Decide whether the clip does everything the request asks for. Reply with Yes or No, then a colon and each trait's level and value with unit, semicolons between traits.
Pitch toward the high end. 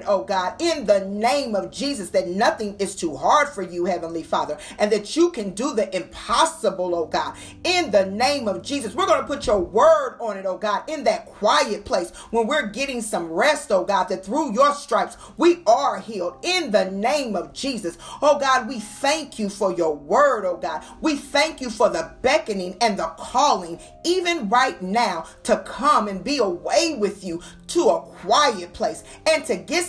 Yes: high, 235 Hz